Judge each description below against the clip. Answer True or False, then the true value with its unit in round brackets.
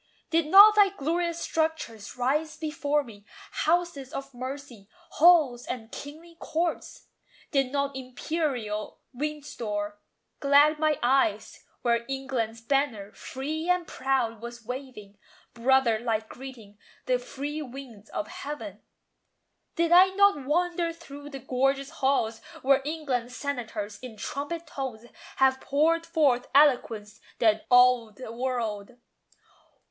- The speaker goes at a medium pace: False (120 wpm)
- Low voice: False (270 Hz)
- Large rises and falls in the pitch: False (4.6 semitones)